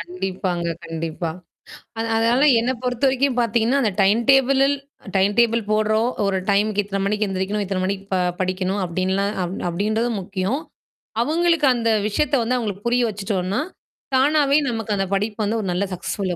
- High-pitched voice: Yes, high, 210 Hz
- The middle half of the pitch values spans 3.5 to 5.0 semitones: Yes, average, 4.0 semitones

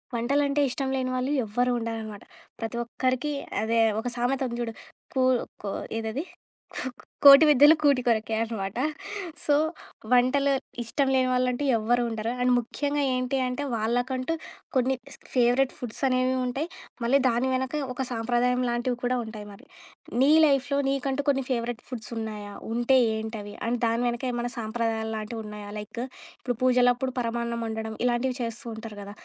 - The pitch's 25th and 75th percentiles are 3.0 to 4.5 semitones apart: No, narrow, 2.5 semitones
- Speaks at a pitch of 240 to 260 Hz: Yes, high, 245 Hz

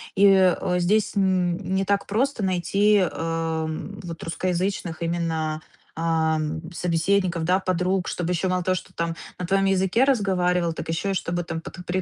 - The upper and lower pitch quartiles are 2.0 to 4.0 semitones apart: Yes, narrow, 2.5 semitones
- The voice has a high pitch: No, medium, 180 Hz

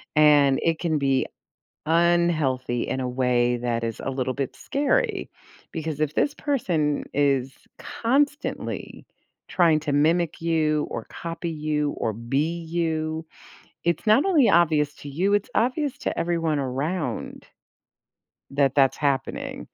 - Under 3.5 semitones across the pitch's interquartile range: No, average, 4.0 semitones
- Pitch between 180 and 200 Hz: No, medium, 155 Hz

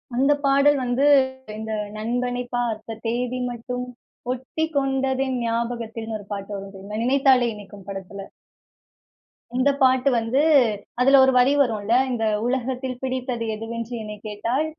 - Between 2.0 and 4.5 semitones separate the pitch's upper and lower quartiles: Yes, average, 2.8 semitones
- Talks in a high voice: Yes, high, 245 Hz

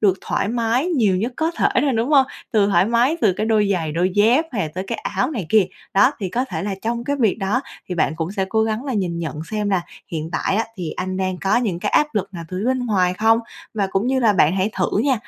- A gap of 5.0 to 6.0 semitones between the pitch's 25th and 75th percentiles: No, average, 4.2 semitones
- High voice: Yes, high, 210 Hz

